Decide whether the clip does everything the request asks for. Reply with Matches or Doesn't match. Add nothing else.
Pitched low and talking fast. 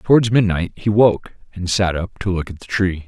Matches